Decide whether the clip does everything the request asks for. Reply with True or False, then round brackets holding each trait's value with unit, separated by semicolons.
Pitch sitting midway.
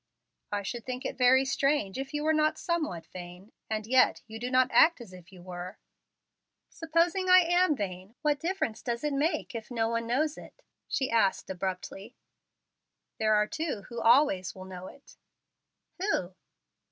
False (240 Hz)